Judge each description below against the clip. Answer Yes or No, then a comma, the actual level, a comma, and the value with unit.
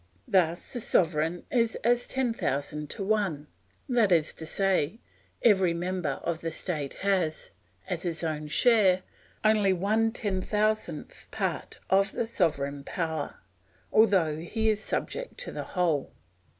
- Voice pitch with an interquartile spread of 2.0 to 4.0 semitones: No, average, 5.1 semitones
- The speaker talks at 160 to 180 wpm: No, average, 140 wpm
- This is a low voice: No, medium, 185 Hz